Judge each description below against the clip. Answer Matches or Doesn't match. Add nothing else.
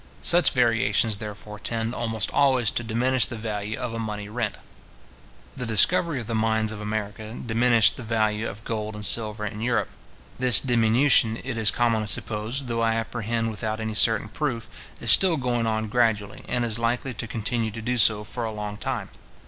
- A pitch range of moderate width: Doesn't match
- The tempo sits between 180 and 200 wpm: Matches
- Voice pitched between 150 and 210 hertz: Doesn't match